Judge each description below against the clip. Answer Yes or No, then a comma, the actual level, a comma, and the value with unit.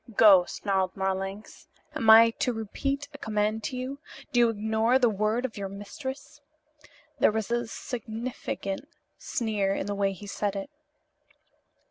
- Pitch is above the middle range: Yes, high, 220 Hz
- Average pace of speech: Yes, average, 150 wpm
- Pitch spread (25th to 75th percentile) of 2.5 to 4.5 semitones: Yes, average, 3.2 semitones